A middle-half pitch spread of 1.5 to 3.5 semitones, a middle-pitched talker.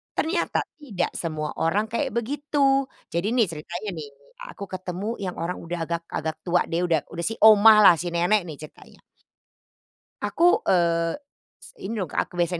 No: average, 4.8 semitones; medium, 180 Hz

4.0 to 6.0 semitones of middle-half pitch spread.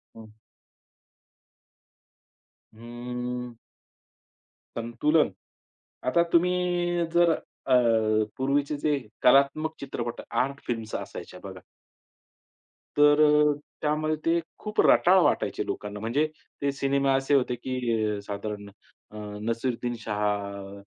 Yes: average, 4.6 semitones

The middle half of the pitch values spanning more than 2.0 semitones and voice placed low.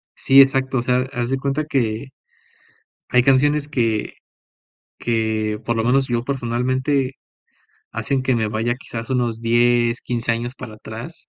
Yes: narrow, 2.4 semitones; low, 120 Hz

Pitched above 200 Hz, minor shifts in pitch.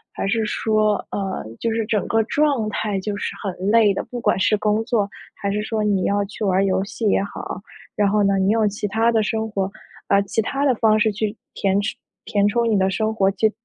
Yes: high, 210 Hz; narrow, 1.9 semitones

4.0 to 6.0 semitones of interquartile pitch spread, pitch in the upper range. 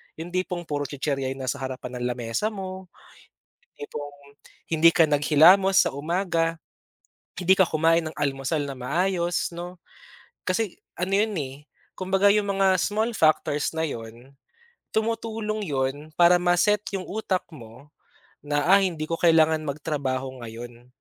No: average, 5.1 semitones; medium, 165 Hz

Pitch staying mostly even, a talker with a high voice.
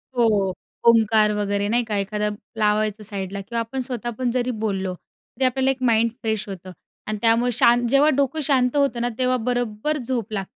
No: average, 3.0 semitones; high, 230 Hz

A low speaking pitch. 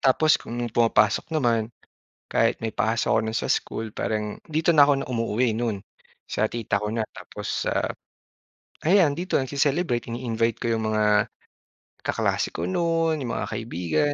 Yes: low, 120 Hz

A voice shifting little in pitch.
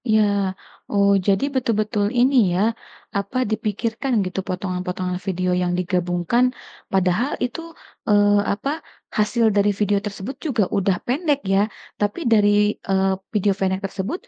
No: average, 3.0 semitones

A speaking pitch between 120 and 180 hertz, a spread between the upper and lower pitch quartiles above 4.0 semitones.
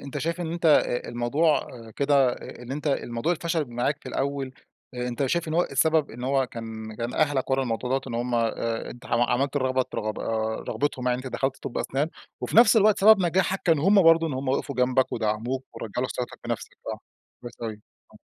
Yes: low, 135 Hz; average, 4.4 semitones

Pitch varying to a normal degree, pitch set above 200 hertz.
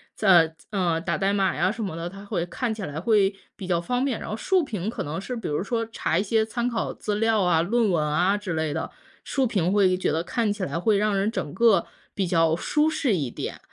No: average, 4.5 semitones; high, 195 Hz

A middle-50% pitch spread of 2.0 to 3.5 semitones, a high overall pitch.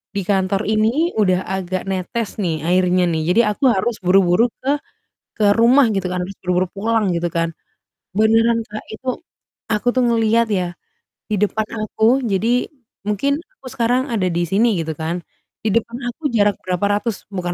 No: average, 4.1 semitones; high, 210 Hz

